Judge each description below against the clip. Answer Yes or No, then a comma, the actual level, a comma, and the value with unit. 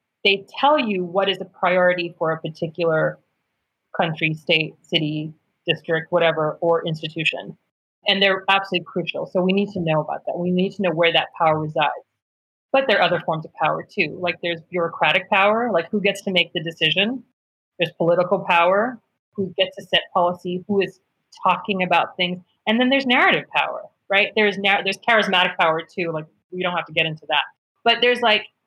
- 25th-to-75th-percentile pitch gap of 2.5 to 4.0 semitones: Yes, average, 2.9 semitones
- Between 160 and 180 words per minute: No, average, 190 wpm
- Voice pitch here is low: No, medium, 180 Hz